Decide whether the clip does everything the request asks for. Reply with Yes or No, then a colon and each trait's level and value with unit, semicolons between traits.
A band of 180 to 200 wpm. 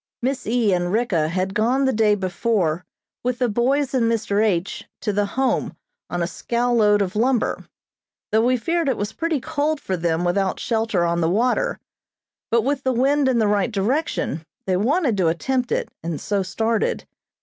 Yes: average, 185 wpm